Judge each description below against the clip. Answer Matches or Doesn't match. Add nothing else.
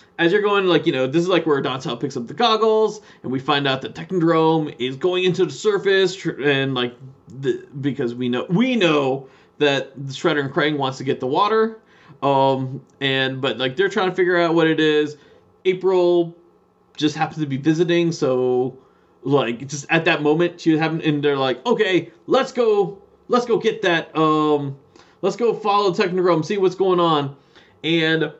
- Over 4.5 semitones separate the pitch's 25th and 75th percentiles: Matches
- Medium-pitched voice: Matches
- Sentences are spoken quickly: Doesn't match